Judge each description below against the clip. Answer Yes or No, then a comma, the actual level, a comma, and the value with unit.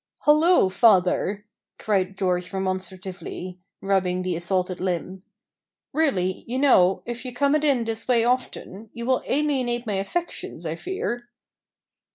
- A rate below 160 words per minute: Yes, slow, 135 wpm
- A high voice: Yes, high, 200 Hz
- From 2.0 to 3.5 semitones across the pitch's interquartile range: No, average, 5.3 semitones